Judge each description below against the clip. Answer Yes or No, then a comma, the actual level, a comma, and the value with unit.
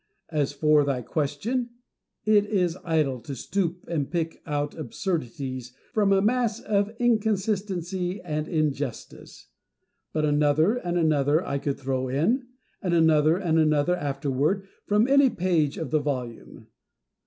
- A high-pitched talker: No, medium, 160 Hz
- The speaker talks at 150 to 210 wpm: No, slow, 135 wpm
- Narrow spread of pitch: No, average, 5.2 semitones